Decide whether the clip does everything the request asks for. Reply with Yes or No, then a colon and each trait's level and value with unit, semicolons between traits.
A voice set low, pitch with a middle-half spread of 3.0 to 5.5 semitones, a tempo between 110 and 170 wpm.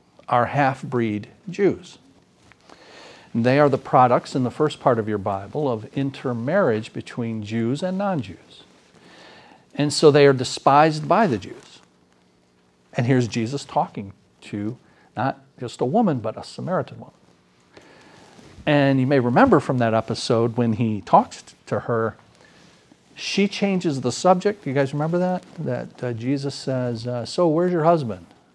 Yes: low, 125 Hz; average, 4.9 semitones; average, 150 wpm